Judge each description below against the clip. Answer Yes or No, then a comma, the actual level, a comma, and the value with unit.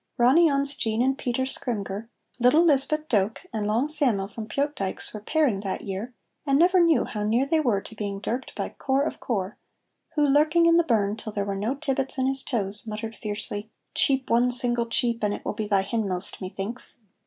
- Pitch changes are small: No, average, 5.0 semitones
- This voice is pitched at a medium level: No, high, 235 Hz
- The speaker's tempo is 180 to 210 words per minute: Yes, average, 200 wpm